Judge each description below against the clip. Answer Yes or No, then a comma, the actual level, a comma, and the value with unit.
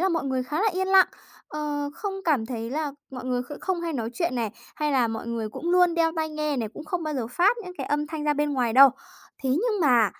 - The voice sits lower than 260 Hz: No, very high, 295 Hz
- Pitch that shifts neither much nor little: Yes, average, 5.0 semitones